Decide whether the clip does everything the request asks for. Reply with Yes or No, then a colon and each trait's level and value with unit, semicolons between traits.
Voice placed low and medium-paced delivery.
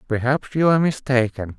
Yes: low, 130 Hz; average, 150 wpm